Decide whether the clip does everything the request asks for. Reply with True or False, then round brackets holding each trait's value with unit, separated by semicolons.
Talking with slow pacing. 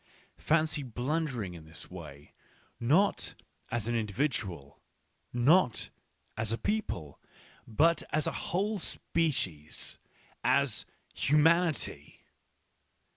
True (90 wpm)